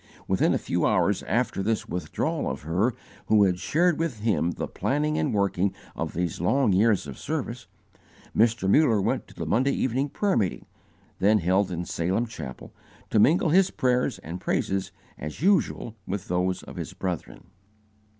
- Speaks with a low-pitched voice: Yes, low, 105 Hz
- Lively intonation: Yes, wide, 6.3 semitones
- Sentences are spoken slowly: No, average, 170 wpm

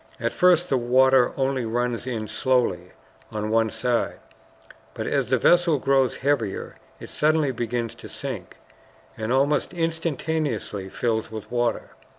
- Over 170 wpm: No, average, 140 wpm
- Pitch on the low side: Yes, low, 125 Hz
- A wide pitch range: No, average, 4.0 semitones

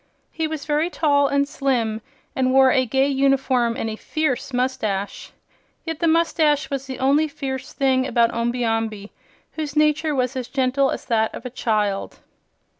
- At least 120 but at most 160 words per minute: No, average, 170 wpm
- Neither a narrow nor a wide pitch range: Yes, average, 3.2 semitones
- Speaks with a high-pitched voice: Yes, very high, 265 Hz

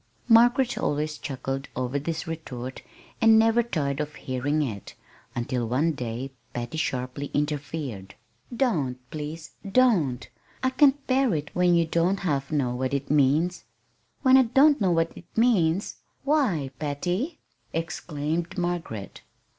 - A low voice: No, medium, 155 Hz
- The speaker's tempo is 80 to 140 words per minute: Yes, slow, 135 wpm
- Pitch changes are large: Yes, wide, 6.4 semitones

